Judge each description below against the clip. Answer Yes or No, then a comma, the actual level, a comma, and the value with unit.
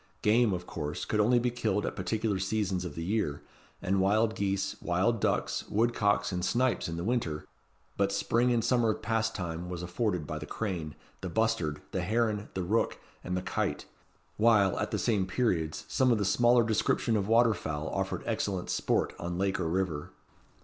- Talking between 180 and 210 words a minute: Yes, average, 185 wpm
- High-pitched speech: No, low, 100 Hz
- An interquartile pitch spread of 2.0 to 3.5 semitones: No, average, 4.1 semitones